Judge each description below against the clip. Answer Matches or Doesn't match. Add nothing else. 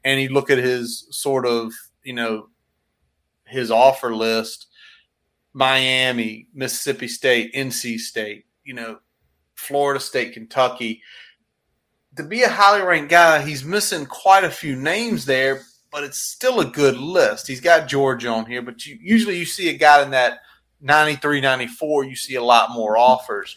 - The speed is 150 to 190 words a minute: Matches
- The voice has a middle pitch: Doesn't match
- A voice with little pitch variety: Doesn't match